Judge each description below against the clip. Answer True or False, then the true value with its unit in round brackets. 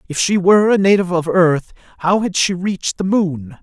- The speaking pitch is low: False (180 Hz)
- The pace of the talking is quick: True (215 wpm)